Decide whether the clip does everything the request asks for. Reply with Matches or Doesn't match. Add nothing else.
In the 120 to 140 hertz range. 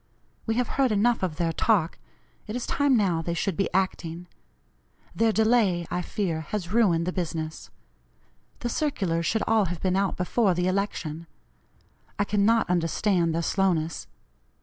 Doesn't match